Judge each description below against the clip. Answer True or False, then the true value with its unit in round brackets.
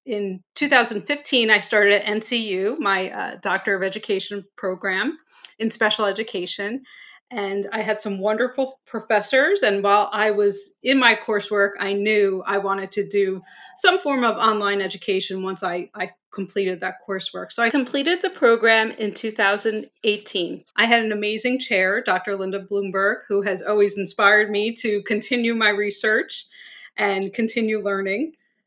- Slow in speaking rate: False (150 wpm)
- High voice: True (210 Hz)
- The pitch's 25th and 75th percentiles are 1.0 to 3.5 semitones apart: True (2.5 semitones)